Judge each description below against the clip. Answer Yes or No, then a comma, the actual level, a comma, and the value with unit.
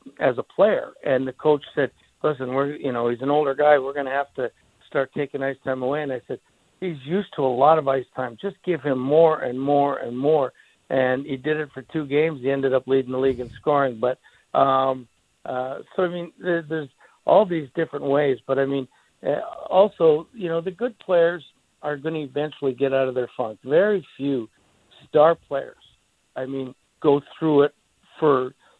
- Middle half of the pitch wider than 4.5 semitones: No, average, 3.2 semitones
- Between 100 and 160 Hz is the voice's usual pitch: Yes, medium, 140 Hz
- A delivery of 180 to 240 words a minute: Yes, fast, 205 wpm